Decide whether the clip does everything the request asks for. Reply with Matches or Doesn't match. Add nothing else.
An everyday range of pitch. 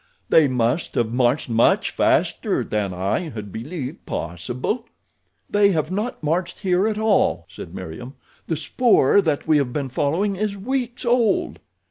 Doesn't match